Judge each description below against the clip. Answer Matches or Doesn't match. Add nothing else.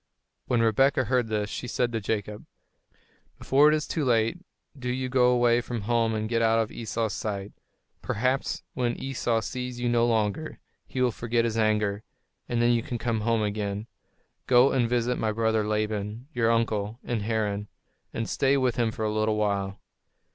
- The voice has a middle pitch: Doesn't match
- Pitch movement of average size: Doesn't match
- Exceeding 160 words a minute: Matches